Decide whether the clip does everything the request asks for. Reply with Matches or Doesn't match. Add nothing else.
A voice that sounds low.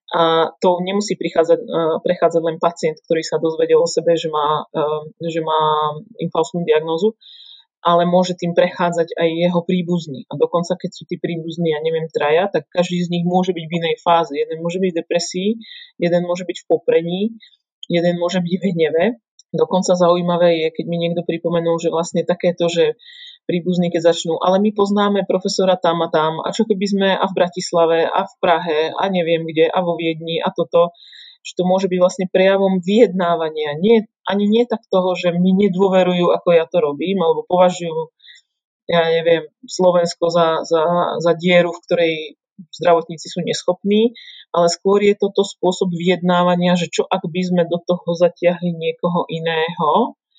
Doesn't match